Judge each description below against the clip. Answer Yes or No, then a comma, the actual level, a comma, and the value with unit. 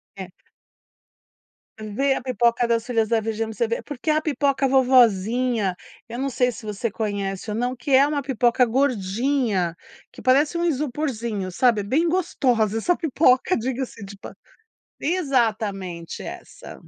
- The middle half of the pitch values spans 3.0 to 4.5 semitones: Yes, average, 4.0 semitones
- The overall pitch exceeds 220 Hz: Yes, high, 240 Hz